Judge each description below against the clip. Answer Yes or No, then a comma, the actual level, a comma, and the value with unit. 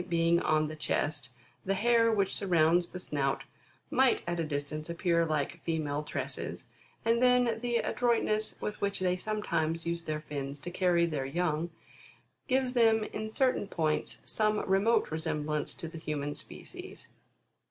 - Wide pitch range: Yes, wide, 5.7 semitones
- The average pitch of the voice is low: No, medium, 170 Hz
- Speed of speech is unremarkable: Yes, average, 155 wpm